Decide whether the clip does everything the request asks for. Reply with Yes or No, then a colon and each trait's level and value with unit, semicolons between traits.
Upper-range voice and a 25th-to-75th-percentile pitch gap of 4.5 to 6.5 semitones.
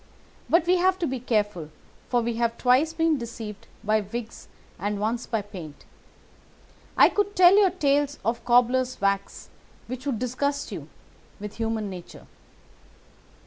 Yes: high, 240 Hz; wide, 5.4 semitones